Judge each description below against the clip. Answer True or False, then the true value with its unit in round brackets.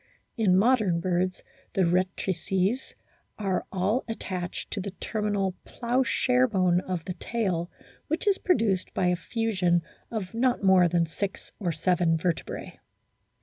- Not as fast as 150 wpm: True (135 wpm)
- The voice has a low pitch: False (190 Hz)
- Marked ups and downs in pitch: False (3.9 semitones)